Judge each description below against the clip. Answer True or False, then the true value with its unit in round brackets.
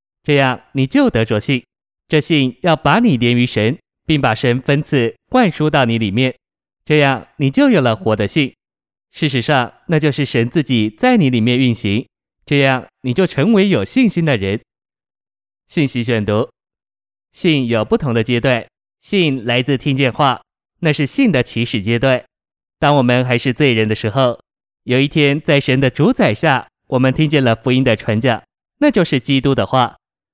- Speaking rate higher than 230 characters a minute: True (240 characters per minute)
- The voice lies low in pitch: True (130 Hz)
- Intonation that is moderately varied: True (3.8 semitones)